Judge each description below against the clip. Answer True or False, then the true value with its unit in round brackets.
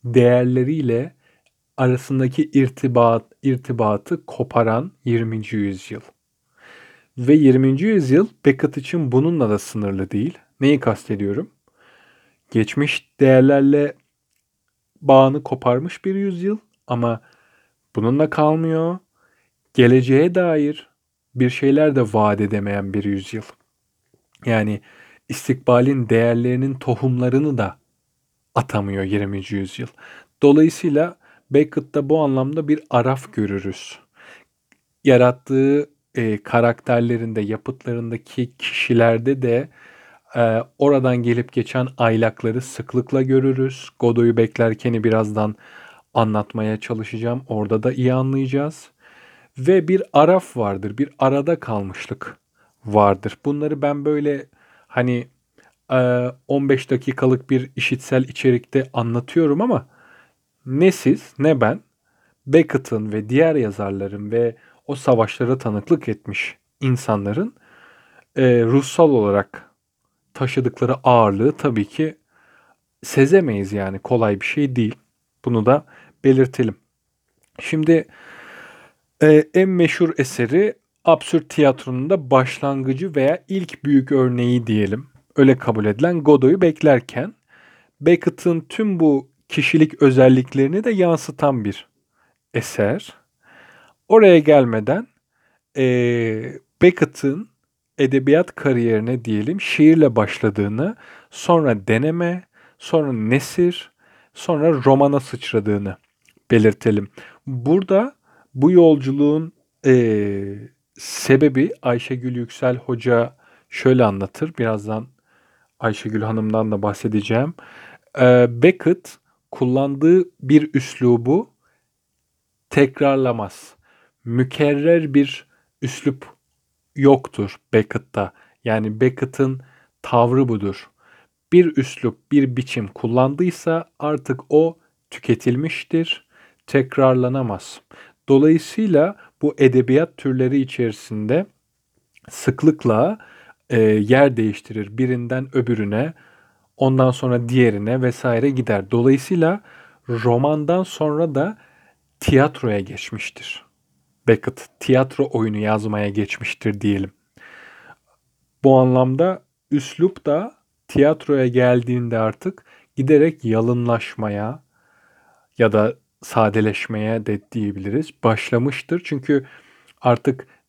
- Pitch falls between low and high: False (130 Hz)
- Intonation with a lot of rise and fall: False (4.3 semitones)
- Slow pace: True (85 wpm)